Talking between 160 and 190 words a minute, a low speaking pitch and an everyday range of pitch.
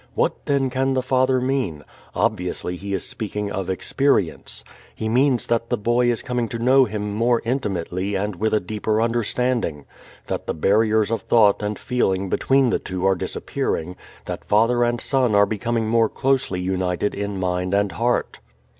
Yes: average, 170 wpm; low, 110 Hz; average, 4.1 semitones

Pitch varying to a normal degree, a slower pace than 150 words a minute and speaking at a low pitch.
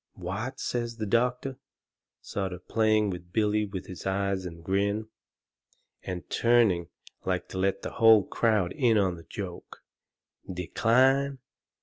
Yes: average, 3.7 semitones; slow, 135 wpm; low, 105 Hz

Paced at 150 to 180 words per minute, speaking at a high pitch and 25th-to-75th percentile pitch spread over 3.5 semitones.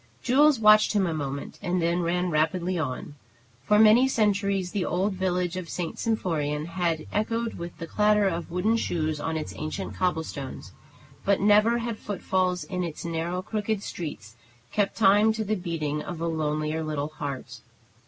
No: average, 170 wpm; medium, 180 Hz; average, 4.5 semitones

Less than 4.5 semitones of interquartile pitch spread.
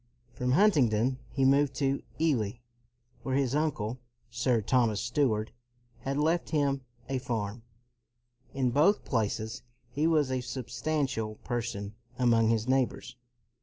Yes: average, 3.4 semitones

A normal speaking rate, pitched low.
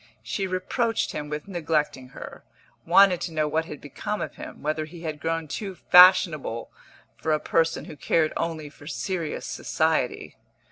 No: average, 160 wpm; medium, 160 Hz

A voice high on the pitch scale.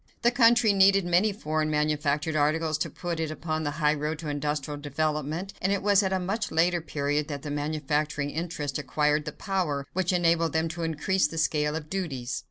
No: medium, 155 Hz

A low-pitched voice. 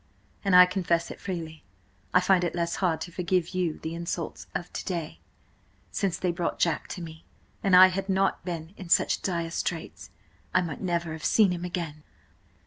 No: medium, 175 Hz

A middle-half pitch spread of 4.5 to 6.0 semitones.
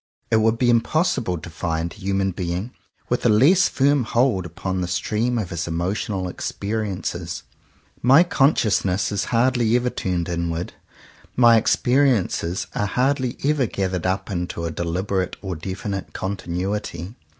Yes: average, 5.2 semitones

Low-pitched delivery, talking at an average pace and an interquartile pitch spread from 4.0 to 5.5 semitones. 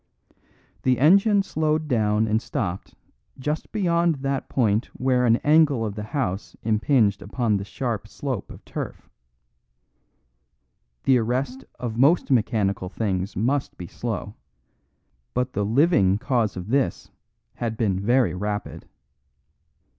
No: low, 120 Hz; slow, 125 wpm; average, 4.8 semitones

